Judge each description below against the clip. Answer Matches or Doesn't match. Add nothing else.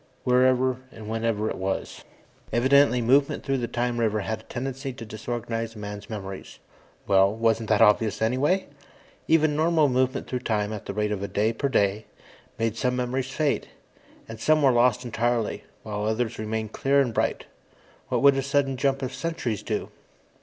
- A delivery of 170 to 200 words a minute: Matches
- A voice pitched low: Matches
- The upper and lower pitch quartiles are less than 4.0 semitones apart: Matches